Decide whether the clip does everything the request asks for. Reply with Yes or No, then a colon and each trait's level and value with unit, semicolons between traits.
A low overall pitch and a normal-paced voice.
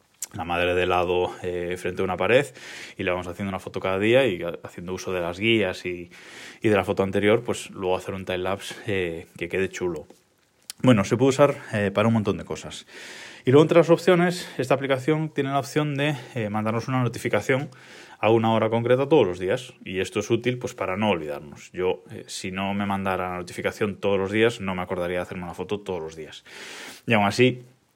No: low, 100 Hz; fast, 220 wpm